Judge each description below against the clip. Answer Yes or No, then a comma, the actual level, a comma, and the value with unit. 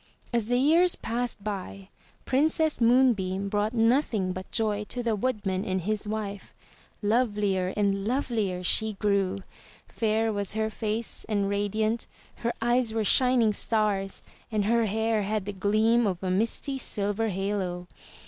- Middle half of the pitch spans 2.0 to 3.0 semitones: Yes, average, 2.7 semitones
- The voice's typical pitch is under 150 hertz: No, high, 215 Hz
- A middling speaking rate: Yes, average, 145 wpm